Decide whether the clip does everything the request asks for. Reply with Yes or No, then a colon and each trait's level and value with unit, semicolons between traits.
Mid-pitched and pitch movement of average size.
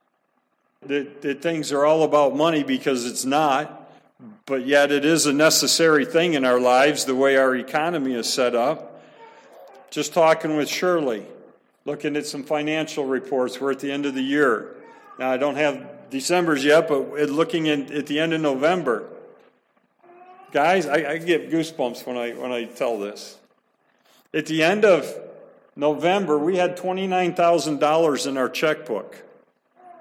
Yes: medium, 150 Hz; average, 3.3 semitones